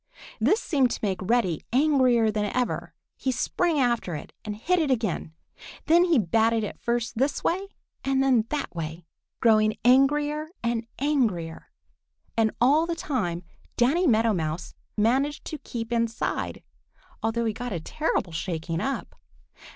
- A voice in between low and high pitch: No, high, 235 Hz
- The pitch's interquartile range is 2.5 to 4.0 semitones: No, average, 4.7 semitones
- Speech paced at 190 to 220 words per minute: No, average, 150 wpm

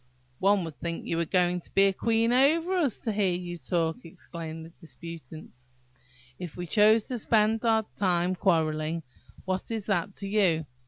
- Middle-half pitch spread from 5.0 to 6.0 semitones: No, average, 4.3 semitones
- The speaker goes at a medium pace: Yes, average, 175 wpm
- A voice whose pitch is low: No, medium, 185 Hz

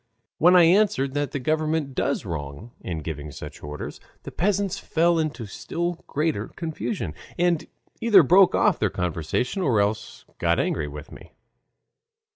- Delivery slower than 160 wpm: Yes, average, 150 wpm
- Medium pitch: Yes, medium, 145 Hz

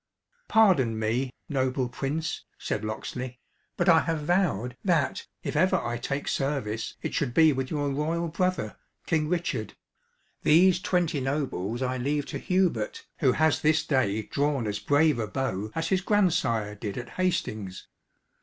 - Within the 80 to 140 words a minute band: No, average, 155 wpm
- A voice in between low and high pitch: Yes, medium, 145 Hz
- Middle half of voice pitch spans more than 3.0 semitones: Yes, wide, 5.5 semitones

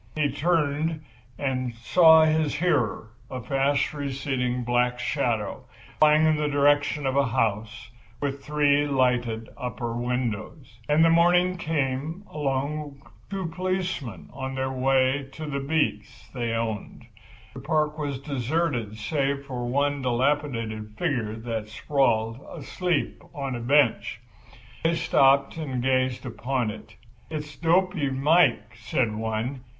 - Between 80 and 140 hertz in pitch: Yes, low, 135 Hz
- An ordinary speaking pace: No, slow, 130 wpm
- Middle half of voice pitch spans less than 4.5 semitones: Yes, average, 3.8 semitones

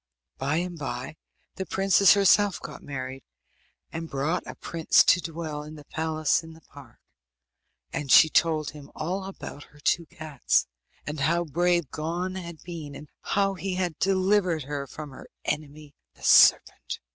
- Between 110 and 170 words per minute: Yes, average, 160 wpm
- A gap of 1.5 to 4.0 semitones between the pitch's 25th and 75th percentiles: Yes, average, 3.3 semitones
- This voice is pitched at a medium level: Yes, medium, 160 Hz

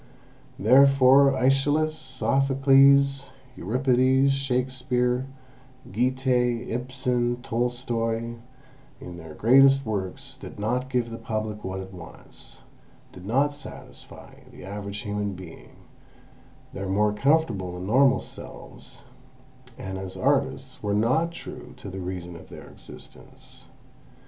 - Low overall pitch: Yes, low, 125 Hz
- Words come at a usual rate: No, slow, 110 wpm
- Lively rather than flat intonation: No, average, 4.6 semitones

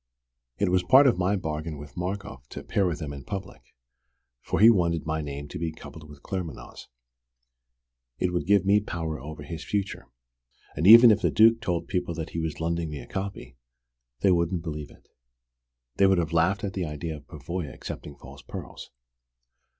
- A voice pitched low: Yes, very low, 85 Hz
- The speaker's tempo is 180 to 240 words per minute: Yes, average, 190 wpm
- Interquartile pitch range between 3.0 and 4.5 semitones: Yes, average, 4.0 semitones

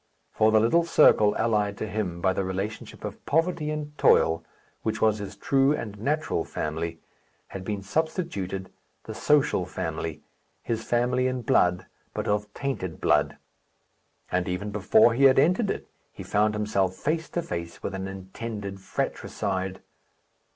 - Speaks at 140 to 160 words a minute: Yes, average, 150 wpm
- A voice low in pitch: Yes, low, 105 Hz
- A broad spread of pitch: Yes, wide, 5.8 semitones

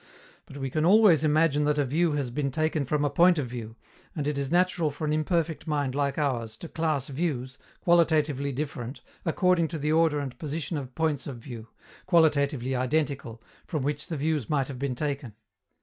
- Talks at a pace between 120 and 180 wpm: No, average, 195 wpm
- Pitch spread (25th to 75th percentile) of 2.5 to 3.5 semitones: Yes, average, 2.9 semitones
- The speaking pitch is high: No, medium, 145 Hz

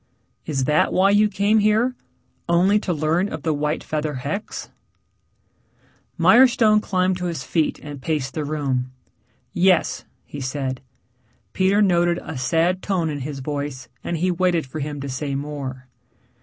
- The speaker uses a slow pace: No, average, 155 wpm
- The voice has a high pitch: No, medium, 160 Hz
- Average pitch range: Yes, average, 4.6 semitones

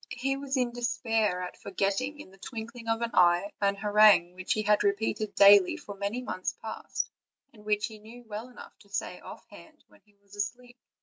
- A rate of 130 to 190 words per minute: No, average, 200 wpm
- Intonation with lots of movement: No, average, 3.0 semitones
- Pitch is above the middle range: Yes, high, 210 Hz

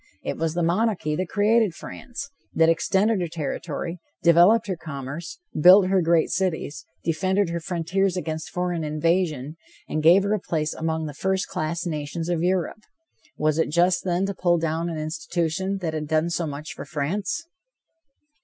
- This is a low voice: No, medium, 170 Hz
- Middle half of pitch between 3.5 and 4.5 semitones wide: No, average, 3.0 semitones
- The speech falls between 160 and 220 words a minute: Yes, average, 170 wpm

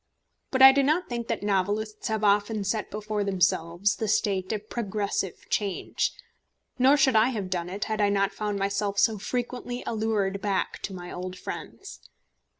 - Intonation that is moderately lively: No, narrow, 2.2 semitones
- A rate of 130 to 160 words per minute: No, average, 170 wpm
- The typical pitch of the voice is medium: No, high, 205 Hz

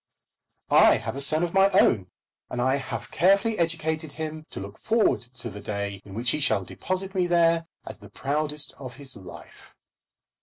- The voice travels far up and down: Yes, wide, 5.8 semitones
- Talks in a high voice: No, medium, 150 Hz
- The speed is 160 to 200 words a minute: Yes, average, 185 wpm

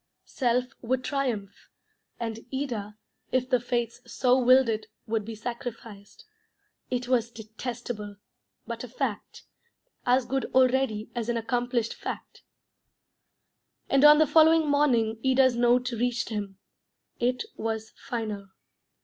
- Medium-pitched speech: No, high, 240 Hz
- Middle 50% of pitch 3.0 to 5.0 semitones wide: No, narrow, 2.6 semitones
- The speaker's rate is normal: No, slow, 125 wpm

